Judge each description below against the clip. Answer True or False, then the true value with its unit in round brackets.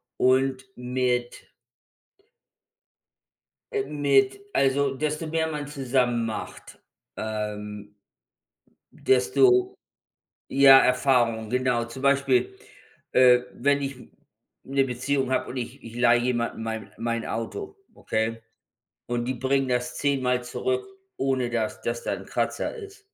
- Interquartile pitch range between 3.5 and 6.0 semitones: False (2.7 semitones)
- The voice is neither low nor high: False (130 Hz)